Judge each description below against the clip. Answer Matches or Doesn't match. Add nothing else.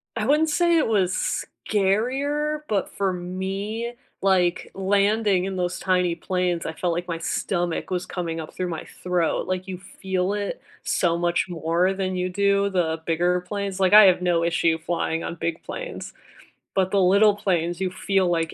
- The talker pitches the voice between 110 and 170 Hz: Doesn't match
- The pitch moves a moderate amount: Doesn't match